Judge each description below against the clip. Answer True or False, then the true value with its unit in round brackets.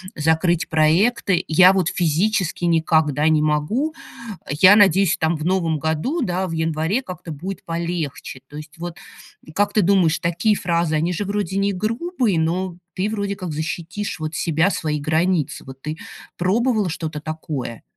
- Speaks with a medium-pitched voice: True (170 Hz)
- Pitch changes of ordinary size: True (3.8 semitones)